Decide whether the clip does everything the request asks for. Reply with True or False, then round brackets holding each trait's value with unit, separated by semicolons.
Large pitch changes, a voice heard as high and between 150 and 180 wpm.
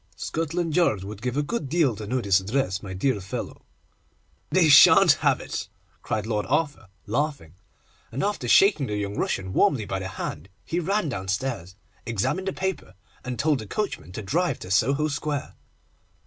False (7.7 semitones; 125 Hz; 175 wpm)